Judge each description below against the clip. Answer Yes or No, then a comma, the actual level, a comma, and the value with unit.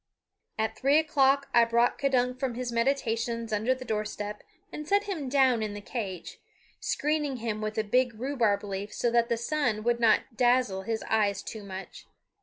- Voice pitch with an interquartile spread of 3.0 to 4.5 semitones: Yes, average, 3.5 semitones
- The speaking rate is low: No, average, 185 wpm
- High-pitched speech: Yes, high, 235 Hz